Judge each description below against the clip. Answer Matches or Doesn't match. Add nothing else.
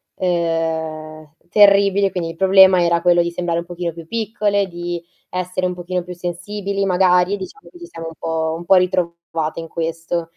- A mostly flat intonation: Matches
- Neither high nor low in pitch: Matches